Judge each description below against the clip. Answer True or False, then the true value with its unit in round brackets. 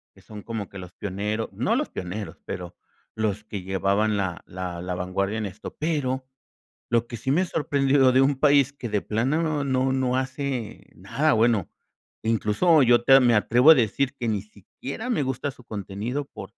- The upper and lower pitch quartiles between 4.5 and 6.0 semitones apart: True (4.8 semitones)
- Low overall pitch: True (115 Hz)